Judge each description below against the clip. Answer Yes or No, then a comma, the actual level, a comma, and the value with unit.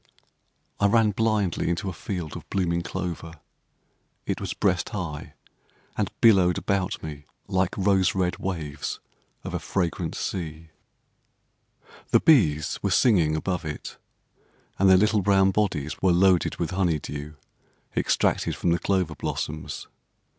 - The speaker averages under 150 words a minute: Yes, slow, 135 wpm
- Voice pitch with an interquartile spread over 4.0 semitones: No, average, 3.4 semitones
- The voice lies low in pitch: Yes, very low, 90 Hz